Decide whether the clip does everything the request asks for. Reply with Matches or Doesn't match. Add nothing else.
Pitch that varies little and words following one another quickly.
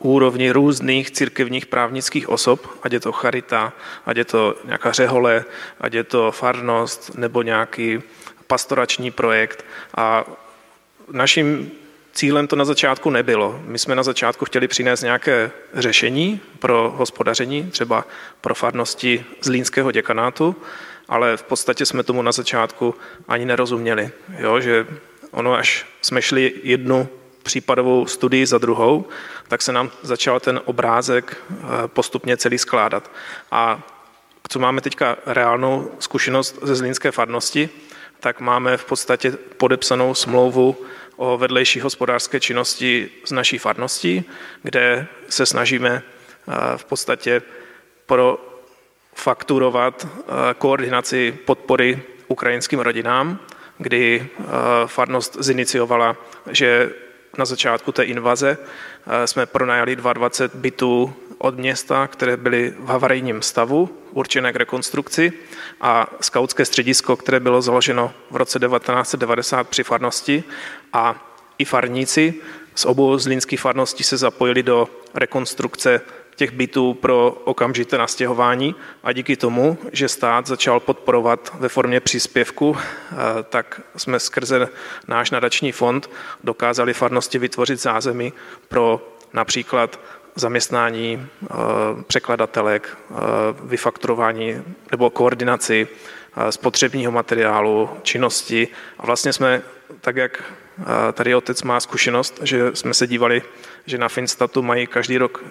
Doesn't match